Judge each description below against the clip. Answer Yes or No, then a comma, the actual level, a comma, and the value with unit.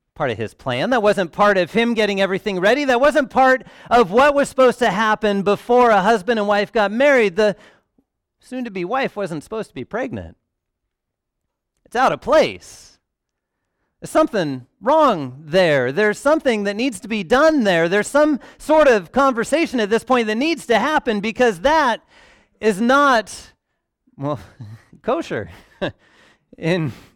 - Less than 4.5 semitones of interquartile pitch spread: No, average, 5.3 semitones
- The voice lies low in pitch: No, high, 220 Hz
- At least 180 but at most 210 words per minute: No, average, 160 wpm